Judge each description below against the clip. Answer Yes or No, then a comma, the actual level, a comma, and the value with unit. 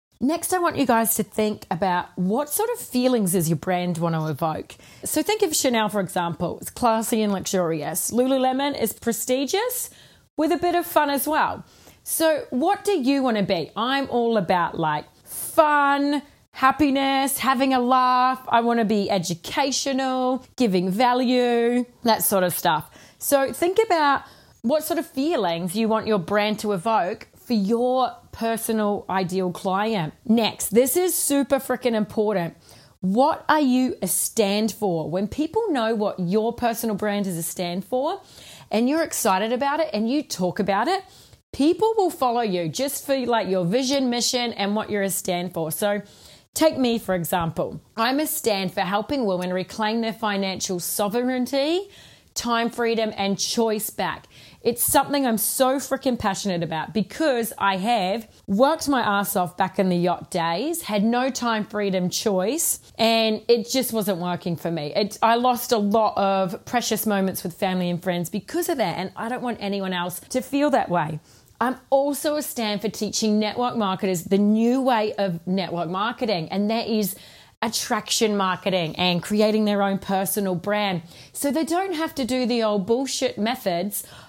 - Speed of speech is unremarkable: Yes, average, 175 wpm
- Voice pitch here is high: Yes, high, 225 Hz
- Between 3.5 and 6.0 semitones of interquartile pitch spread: Yes, wide, 5.4 semitones